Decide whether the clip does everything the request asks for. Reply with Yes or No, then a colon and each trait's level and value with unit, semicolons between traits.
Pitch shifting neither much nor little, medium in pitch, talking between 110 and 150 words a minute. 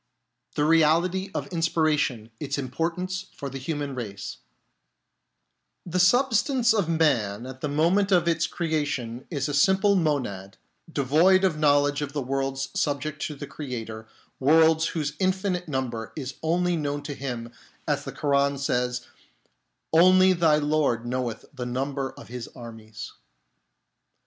Yes: average, 4.5 semitones; medium, 145 Hz; average, 140 wpm